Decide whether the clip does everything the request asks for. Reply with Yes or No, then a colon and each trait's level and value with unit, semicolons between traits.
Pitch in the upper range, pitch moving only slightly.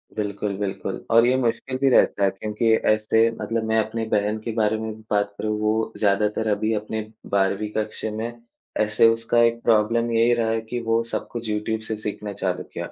No: low, 110 Hz; narrow, 1.4 semitones